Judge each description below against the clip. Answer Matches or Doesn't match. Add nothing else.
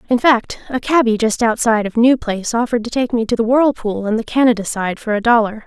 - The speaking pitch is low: Doesn't match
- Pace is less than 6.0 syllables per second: Doesn't match